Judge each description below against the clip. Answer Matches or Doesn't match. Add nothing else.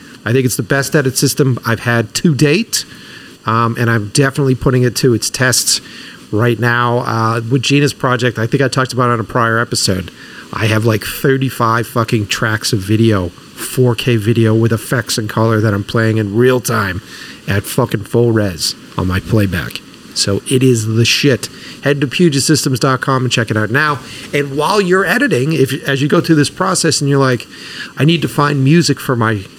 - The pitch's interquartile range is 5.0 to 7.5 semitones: Doesn't match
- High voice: Doesn't match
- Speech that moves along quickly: Doesn't match